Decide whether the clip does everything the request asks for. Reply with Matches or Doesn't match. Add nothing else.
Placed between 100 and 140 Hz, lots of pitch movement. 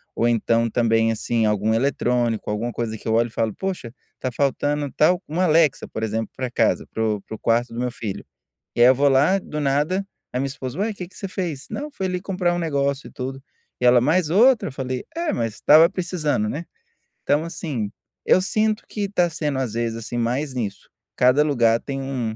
Matches